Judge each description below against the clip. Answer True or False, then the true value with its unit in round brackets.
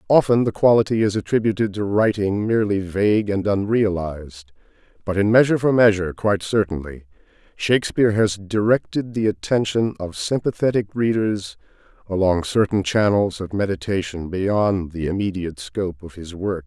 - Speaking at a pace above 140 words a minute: False (135 wpm)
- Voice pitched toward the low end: True (100 Hz)